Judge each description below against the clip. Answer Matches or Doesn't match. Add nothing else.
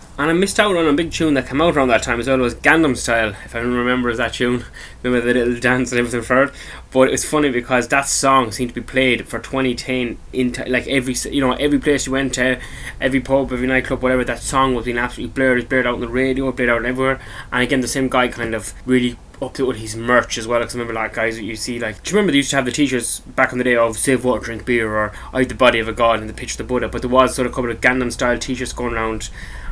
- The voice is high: Doesn't match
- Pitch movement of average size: Doesn't match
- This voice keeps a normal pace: Doesn't match